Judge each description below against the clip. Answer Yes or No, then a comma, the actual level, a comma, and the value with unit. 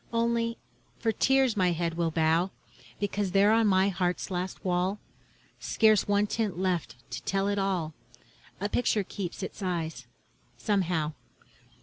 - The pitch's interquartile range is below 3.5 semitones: Yes, average, 2.9 semitones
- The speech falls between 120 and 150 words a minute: Yes, average, 140 wpm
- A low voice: No, high, 190 Hz